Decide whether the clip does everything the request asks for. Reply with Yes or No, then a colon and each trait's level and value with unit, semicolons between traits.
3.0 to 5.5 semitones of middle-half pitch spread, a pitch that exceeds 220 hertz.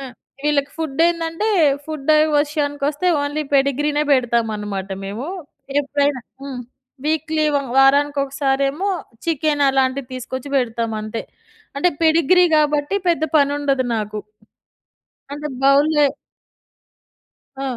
No: narrow, 2.4 semitones; very high, 285 Hz